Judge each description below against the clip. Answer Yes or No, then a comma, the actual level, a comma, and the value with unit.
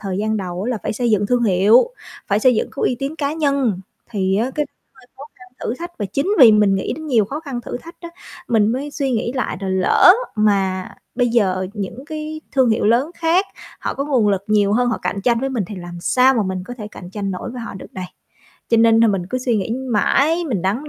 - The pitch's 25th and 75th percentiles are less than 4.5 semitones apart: No, average, 5.1 semitones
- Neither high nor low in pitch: No, high, 230 Hz